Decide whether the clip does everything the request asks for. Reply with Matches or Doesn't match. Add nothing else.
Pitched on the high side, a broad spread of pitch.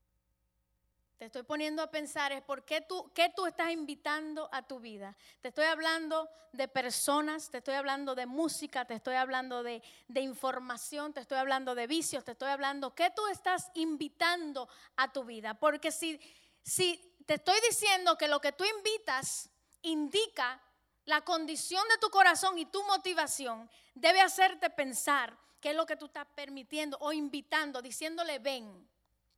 Doesn't match